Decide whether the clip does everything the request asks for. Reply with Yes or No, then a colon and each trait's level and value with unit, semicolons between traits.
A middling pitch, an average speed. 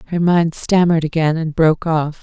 Yes: medium, 160 Hz; average, 190 wpm